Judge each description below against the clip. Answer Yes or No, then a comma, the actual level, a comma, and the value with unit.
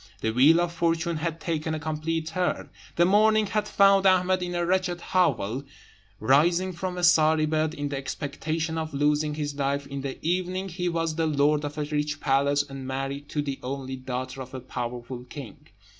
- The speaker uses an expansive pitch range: No, average, 3.8 semitones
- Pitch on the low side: No, medium, 155 Hz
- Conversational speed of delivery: Yes, average, 190 wpm